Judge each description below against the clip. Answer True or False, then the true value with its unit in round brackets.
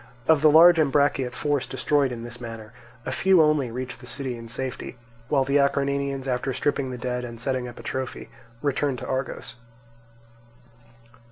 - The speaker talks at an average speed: True (170 wpm)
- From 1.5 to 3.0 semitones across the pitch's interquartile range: True (2.4 semitones)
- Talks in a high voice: False (130 Hz)